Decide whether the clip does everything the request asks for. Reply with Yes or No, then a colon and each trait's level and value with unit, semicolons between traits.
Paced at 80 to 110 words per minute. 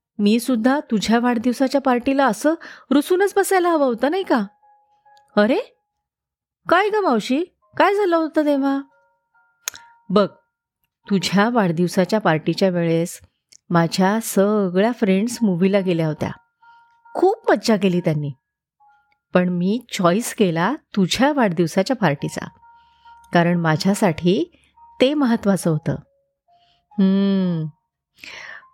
Yes: average, 100 wpm